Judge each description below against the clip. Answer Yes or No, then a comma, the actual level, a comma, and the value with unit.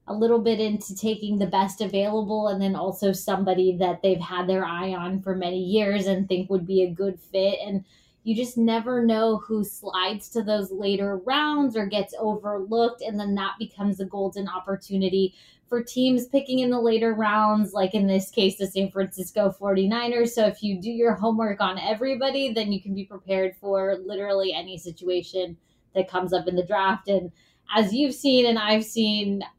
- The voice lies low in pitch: No, high, 200 Hz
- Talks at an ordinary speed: Yes, average, 190 wpm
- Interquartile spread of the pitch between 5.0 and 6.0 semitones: No, narrow, 2.4 semitones